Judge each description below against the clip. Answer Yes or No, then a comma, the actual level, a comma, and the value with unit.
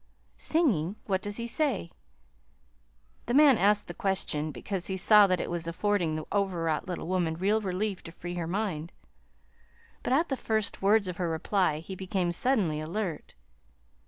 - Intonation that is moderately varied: Yes, average, 3.8 semitones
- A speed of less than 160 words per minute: No, average, 165 wpm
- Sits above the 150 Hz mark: Yes, high, 190 Hz